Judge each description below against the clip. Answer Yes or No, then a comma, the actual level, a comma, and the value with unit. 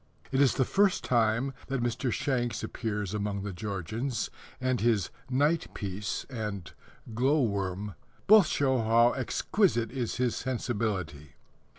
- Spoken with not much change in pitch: No, average, 4.3 semitones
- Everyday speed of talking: No, slow, 130 wpm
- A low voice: Yes, low, 115 Hz